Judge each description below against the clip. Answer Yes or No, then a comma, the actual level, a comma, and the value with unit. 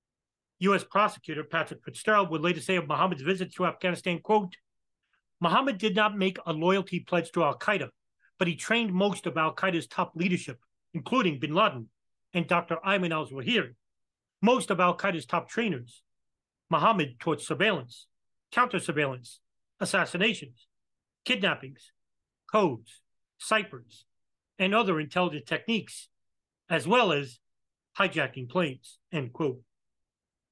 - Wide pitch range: Yes, wide, 5.7 semitones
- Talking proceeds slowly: Yes, slow, 120 wpm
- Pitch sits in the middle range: Yes, medium, 170 Hz